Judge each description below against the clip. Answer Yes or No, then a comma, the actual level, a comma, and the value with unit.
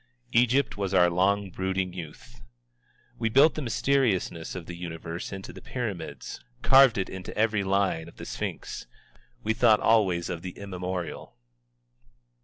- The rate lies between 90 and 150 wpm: Yes, average, 145 wpm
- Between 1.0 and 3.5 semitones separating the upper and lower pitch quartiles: No, average, 4.3 semitones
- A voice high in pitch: No, very low, 95 Hz